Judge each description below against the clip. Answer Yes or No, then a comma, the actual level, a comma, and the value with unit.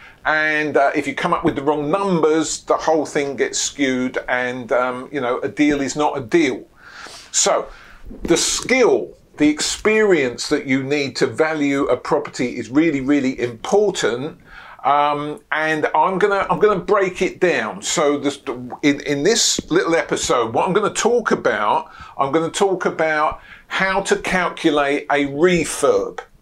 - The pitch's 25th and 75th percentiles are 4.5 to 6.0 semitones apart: Yes, average, 4.8 semitones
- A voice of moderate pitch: Yes, medium, 155 Hz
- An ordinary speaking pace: Yes, average, 160 wpm